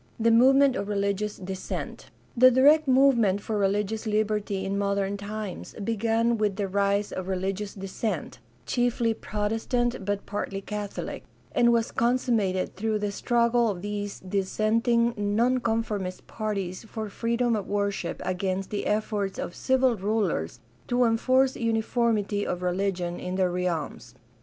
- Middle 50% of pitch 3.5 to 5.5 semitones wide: No, average, 2.8 semitones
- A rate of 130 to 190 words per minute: Yes, average, 140 wpm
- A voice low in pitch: No, high, 210 Hz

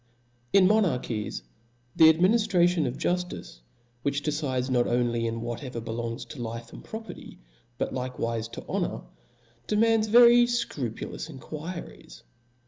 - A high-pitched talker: No, medium, 140 Hz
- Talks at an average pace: No, slow, 120 wpm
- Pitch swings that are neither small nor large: No, wide, 7.7 semitones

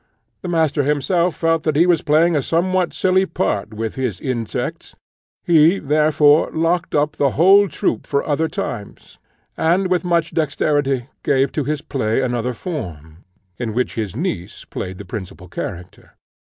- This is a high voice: No, medium, 145 Hz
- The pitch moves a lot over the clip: Yes, wide, 5.9 semitones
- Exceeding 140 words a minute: Yes, average, 155 wpm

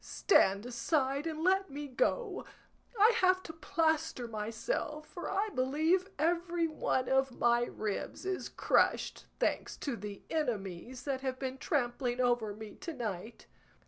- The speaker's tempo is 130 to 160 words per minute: Yes, average, 145 wpm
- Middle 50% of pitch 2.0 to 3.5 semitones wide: No, wide, 5.6 semitones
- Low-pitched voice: No, very high, 270 Hz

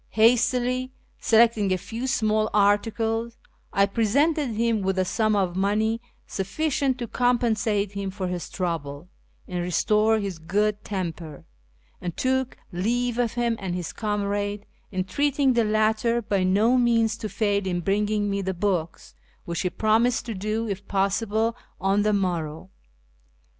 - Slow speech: No, average, 145 wpm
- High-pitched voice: Yes, high, 210 Hz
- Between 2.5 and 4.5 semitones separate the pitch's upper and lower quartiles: Yes, average, 3.2 semitones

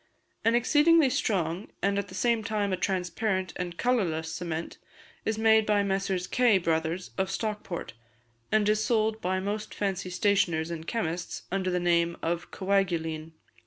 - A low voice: No, high, 190 Hz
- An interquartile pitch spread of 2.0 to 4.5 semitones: Yes, average, 3.9 semitones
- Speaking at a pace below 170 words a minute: Yes, average, 155 wpm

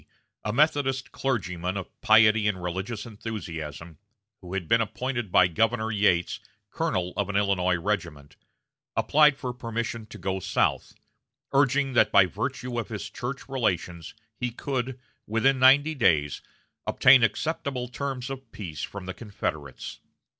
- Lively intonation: Yes, wide, 5.7 semitones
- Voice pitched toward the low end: Yes, low, 110 Hz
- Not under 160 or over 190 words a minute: No, average, 140 wpm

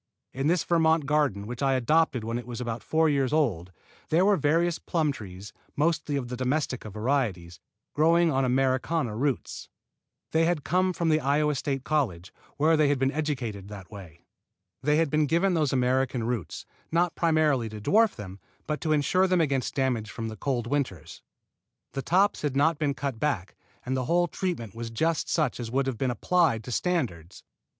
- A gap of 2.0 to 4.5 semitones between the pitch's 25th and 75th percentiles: No, average, 5.2 semitones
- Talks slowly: No, average, 185 wpm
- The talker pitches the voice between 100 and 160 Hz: Yes, medium, 140 Hz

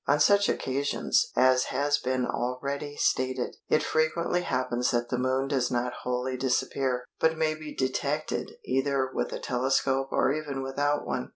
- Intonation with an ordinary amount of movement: No, narrow, 2.3 semitones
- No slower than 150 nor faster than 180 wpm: Yes, average, 160 wpm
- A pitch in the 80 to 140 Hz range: Yes, low, 135 Hz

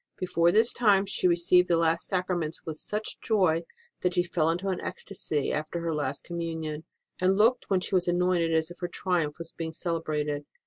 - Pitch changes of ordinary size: No, narrow, 2.3 semitones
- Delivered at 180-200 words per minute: Yes, average, 195 wpm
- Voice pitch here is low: No, medium, 170 Hz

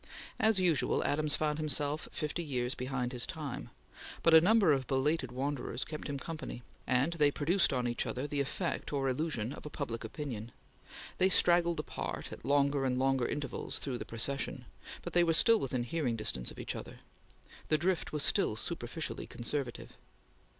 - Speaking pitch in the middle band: Yes, medium, 145 Hz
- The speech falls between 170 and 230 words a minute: Yes, average, 175 wpm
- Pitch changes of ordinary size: Yes, average, 3.9 semitones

